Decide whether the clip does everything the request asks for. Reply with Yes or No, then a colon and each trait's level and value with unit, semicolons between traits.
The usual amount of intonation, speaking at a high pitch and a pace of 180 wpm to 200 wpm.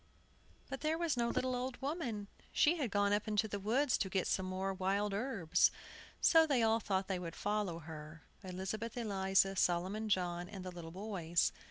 Yes: average, 4.0 semitones; high, 200 Hz; average, 185 wpm